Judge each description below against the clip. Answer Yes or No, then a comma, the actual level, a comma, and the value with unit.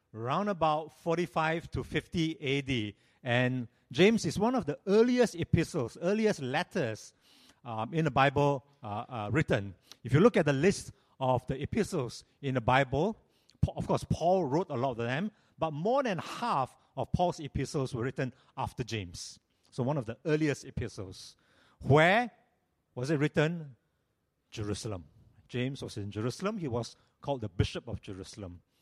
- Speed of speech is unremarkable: Yes, average, 160 wpm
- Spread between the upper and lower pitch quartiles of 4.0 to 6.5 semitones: Yes, wide, 5.6 semitones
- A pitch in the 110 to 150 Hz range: Yes, medium, 140 Hz